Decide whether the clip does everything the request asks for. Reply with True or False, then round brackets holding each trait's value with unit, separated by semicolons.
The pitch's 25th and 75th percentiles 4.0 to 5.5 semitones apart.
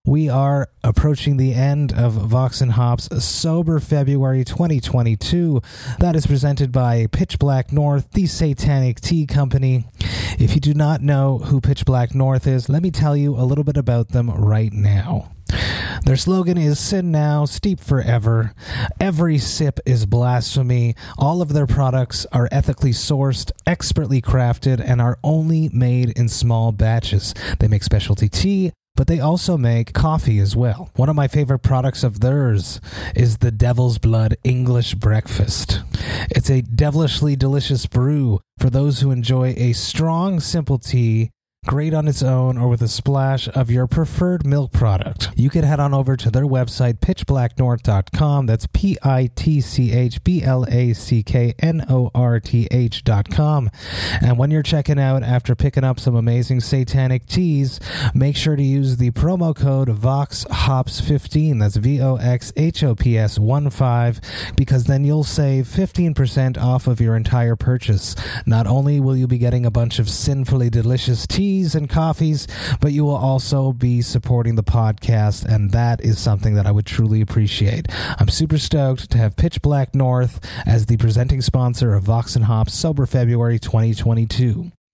False (3.6 semitones)